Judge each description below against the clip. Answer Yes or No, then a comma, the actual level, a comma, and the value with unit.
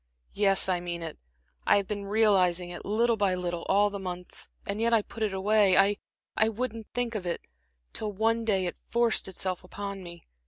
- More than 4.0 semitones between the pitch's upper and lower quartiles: No, average, 3.0 semitones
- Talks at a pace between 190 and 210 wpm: Yes, average, 195 wpm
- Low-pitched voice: No, high, 200 Hz